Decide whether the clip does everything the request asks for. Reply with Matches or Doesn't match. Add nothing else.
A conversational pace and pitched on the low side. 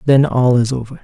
Doesn't match